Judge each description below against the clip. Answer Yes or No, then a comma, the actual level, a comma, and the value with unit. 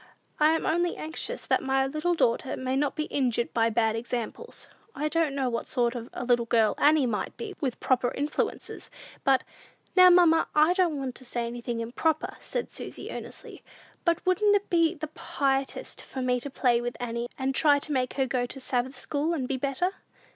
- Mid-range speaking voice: No, very high, 270 Hz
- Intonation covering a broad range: No, average, 4.4 semitones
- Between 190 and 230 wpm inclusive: Yes, average, 200 wpm